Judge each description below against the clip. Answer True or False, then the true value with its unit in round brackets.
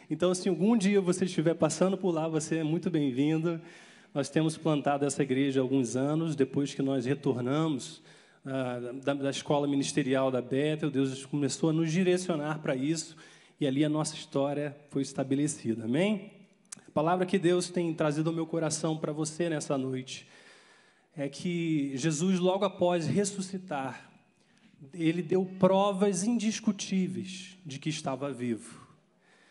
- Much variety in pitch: False (4.6 semitones)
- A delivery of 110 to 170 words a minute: True (155 wpm)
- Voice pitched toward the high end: False (160 Hz)